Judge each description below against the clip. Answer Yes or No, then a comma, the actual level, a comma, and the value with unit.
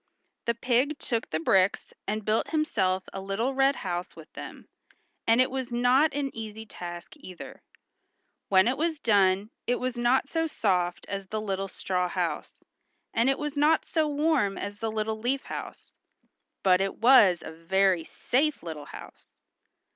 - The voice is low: No, high, 220 Hz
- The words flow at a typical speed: Yes, average, 165 wpm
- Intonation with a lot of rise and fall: Yes, wide, 5.8 semitones